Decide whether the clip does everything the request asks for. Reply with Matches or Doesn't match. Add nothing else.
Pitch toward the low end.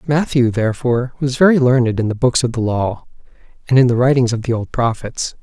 Matches